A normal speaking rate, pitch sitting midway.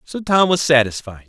Yes: average, 190 wpm; medium, 145 Hz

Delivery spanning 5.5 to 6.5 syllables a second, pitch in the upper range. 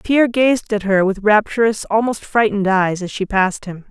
No: 5.3 syllables/s; high, 210 Hz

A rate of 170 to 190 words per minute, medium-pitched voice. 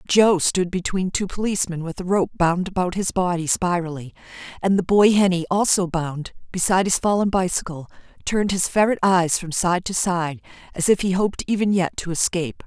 Yes: average, 185 wpm; medium, 180 Hz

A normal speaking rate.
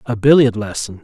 Yes: average, 175 wpm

